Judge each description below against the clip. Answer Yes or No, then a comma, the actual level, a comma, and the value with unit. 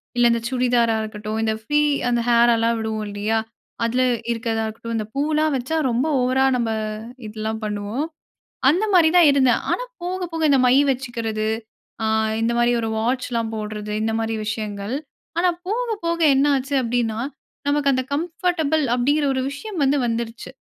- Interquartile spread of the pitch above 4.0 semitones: Yes, average, 4.4 semitones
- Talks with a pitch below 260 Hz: Yes, high, 240 Hz